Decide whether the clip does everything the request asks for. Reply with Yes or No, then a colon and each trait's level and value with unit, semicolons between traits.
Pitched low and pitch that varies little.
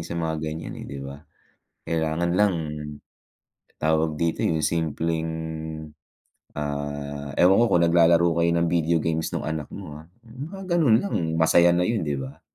Yes: very low, 80 Hz; narrow, 2.0 semitones